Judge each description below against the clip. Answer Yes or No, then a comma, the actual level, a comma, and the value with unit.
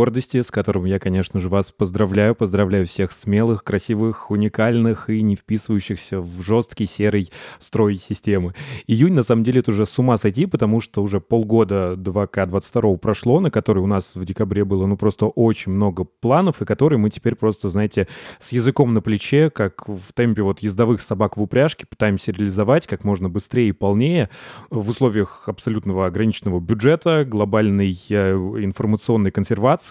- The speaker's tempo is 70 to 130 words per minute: No, fast, 160 wpm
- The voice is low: Yes, low, 105 Hz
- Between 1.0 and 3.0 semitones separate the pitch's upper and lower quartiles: Yes, average, 2.7 semitones